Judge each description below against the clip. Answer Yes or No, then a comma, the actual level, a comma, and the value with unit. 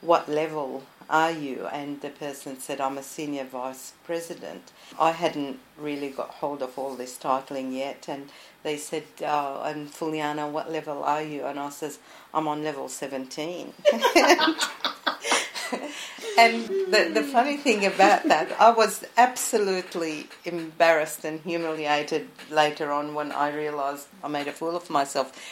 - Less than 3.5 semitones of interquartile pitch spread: Yes, average, 3.1 semitones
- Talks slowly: No, average, 150 wpm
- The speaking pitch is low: No, medium, 150 Hz